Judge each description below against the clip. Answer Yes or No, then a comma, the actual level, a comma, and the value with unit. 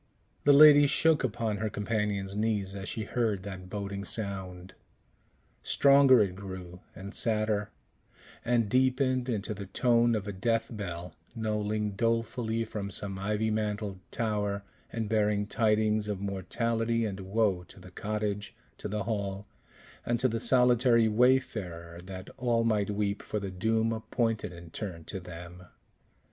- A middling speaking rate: Yes, average, 145 wpm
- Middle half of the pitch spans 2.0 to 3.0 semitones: Yes, narrow, 2.6 semitones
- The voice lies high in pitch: No, low, 105 Hz